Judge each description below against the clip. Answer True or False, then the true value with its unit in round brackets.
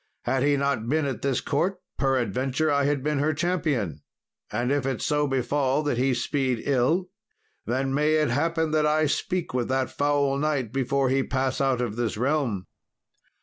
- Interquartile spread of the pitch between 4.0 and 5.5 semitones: False (2.7 semitones)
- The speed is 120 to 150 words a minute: False (180 wpm)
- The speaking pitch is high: False (135 Hz)